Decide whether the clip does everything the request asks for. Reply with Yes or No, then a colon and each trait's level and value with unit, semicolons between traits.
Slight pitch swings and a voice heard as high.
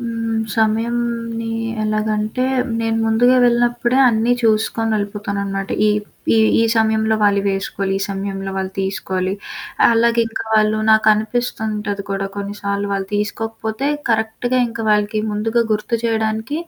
Yes: narrow, 2.0 semitones; high, 220 Hz